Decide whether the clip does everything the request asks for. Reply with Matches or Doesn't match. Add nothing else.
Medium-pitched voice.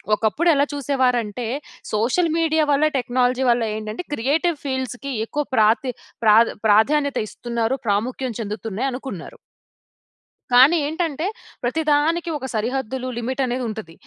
Doesn't match